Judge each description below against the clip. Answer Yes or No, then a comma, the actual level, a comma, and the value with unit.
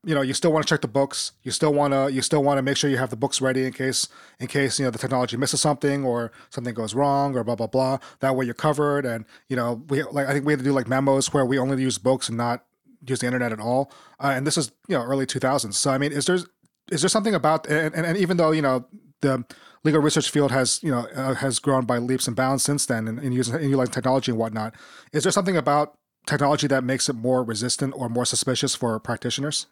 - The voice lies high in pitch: No, low, 135 Hz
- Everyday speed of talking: No, fast, 265 wpm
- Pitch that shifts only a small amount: Yes, narrow, 2.3 semitones